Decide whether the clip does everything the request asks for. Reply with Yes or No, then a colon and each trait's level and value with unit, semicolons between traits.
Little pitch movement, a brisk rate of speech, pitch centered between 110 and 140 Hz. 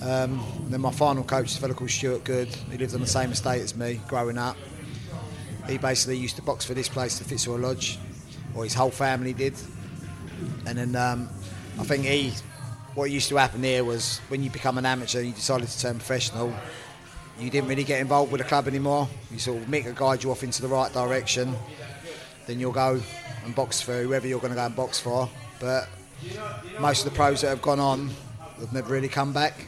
Yes: narrow, 1.8 semitones; fast, 220 wpm; low, 130 Hz